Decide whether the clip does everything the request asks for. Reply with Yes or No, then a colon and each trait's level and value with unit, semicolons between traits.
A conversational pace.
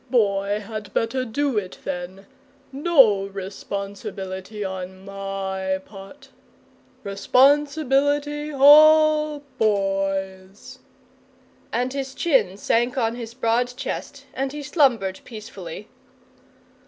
No: slow, 90 wpm